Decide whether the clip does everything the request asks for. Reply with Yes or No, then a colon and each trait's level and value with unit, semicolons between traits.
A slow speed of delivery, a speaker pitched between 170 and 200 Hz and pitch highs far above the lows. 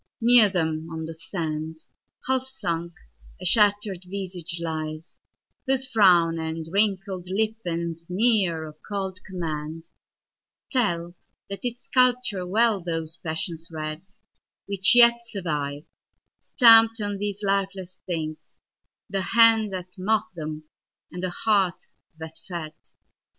No: slow, 110 wpm; medium, 185 Hz; average, 4.2 semitones